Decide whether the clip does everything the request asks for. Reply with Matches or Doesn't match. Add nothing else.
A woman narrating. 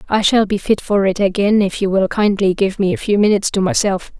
Matches